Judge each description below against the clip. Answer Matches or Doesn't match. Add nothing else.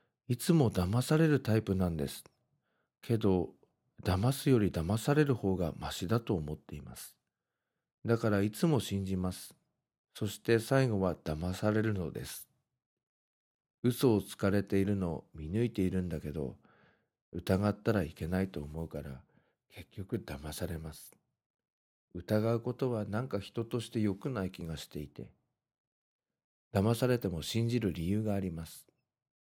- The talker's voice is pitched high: Doesn't match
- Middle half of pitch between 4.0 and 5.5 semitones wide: Matches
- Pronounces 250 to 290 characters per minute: Matches